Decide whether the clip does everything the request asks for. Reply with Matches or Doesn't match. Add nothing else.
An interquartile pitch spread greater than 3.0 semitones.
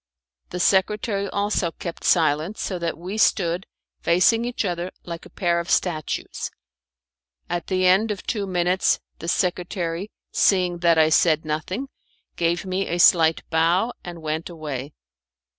Doesn't match